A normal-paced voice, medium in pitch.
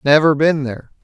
Yes: average, 175 wpm; medium, 145 Hz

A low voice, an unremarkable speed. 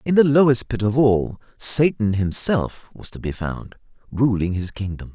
Yes: low, 115 Hz; average, 175 wpm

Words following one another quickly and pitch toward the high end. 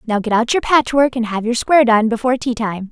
Yes: fast, 245 wpm; high, 235 Hz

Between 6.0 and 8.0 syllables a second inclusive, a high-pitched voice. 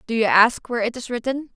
Yes: 6.4 syllables/s; high, 235 Hz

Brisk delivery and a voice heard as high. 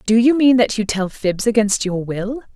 Yes: fast, 235 wpm; high, 220 Hz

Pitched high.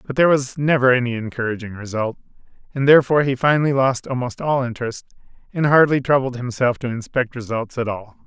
No: low, 125 Hz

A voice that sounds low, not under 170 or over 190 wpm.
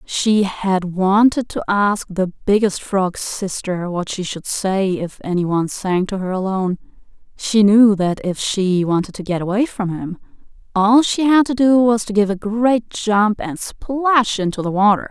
No: high, 200 Hz; average, 185 wpm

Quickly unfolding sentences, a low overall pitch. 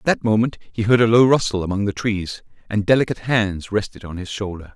Yes: fast, 225 wpm; low, 105 Hz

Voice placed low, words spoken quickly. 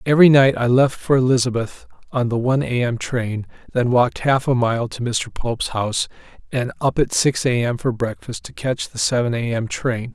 Yes: low, 125 Hz; fast, 215 wpm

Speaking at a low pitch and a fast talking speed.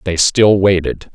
No: very low, 90 Hz; average, 155 wpm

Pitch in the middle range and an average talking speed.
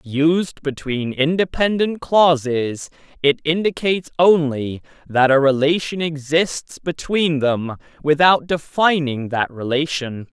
No: medium, 150 Hz; slow, 100 wpm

